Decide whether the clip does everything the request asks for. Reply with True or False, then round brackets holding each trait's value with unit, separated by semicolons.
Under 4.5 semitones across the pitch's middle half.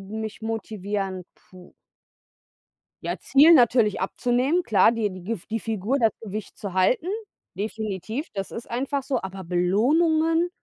False (5.0 semitones)